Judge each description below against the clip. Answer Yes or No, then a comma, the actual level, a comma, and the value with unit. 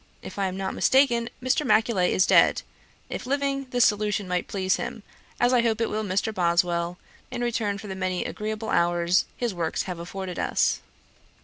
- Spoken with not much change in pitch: No, average, 4.4 semitones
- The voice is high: Yes, high, 205 Hz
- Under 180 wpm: No, average, 185 wpm